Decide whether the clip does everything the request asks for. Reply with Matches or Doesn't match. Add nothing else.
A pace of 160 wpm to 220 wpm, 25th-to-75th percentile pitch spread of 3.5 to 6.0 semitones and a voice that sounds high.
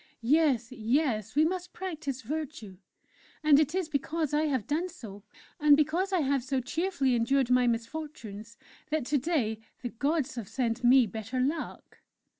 Matches